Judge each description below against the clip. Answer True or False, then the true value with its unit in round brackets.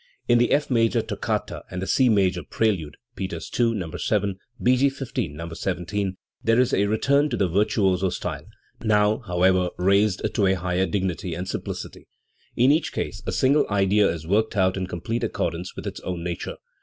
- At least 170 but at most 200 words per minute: True (185 wpm)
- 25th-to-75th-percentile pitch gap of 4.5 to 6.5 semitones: False (3.8 semitones)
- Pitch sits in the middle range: False (100 Hz)